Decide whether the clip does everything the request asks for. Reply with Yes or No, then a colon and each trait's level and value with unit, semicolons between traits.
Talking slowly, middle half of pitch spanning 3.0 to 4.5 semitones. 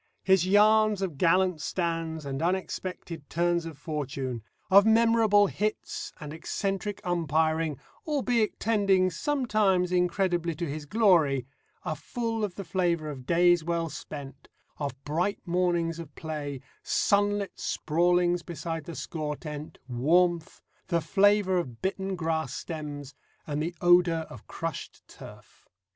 Yes: slow, 130 wpm; average, 3.7 semitones